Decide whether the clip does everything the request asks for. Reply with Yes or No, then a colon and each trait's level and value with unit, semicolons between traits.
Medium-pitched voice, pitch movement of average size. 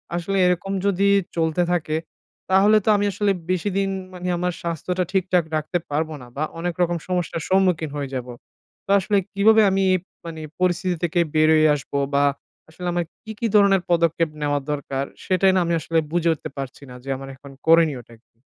Yes: medium, 175 Hz; average, 3.4 semitones